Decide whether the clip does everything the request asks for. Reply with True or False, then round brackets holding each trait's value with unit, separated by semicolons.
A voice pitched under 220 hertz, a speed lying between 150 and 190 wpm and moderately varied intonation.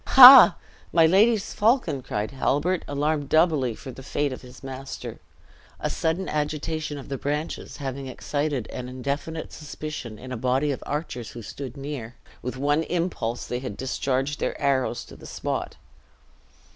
True (140 Hz; 160 wpm; 3.3 semitones)